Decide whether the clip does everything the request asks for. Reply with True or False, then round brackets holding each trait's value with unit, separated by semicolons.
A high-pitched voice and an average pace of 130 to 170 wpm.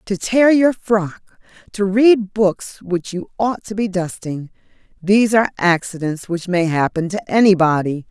True (195 Hz; 155 wpm)